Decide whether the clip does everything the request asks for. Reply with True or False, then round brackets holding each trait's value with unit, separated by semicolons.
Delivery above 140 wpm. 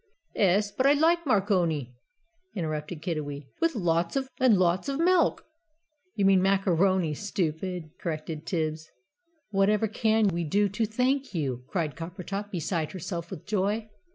False (135 wpm)